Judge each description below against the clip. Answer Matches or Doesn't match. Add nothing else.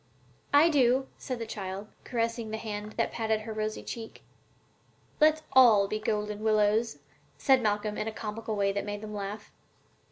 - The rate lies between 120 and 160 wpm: Doesn't match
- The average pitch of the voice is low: Doesn't match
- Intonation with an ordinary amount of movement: Doesn't match